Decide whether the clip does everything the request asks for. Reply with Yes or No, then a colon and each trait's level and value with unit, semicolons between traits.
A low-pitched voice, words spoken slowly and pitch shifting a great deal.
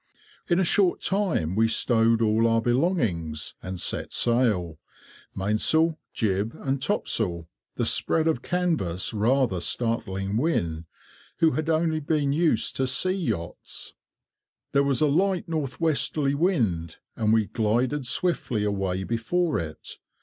Yes: low, 120 Hz; slow, 130 wpm; wide, 7.8 semitones